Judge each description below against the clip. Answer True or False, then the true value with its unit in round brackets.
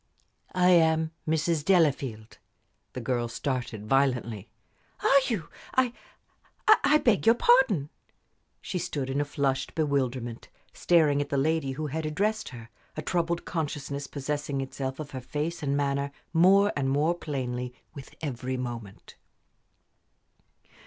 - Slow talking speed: True (130 wpm)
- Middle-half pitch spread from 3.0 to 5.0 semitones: True (4.0 semitones)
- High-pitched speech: False (145 Hz)